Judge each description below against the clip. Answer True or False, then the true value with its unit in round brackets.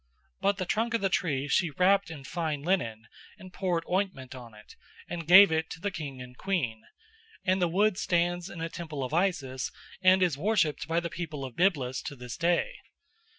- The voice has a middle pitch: True (170 Hz)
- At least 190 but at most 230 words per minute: True (195 wpm)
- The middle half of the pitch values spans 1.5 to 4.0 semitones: False (5.2 semitones)